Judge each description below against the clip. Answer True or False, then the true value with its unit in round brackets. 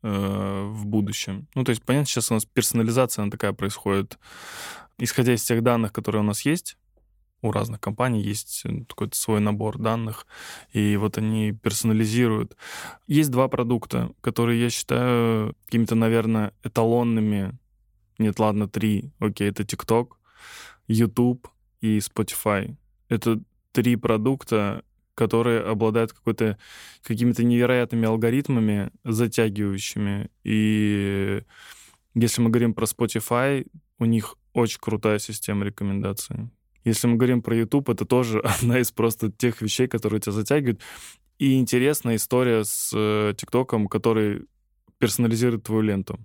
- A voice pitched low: True (110 Hz)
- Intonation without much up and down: True (2.3 semitones)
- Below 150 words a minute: True (125 wpm)